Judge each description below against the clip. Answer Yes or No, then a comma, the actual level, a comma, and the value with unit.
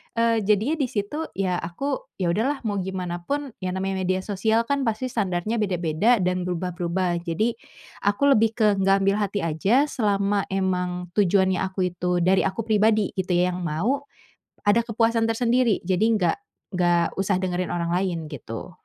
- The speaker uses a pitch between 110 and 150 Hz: No, high, 195 Hz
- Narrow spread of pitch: No, average, 3.8 semitones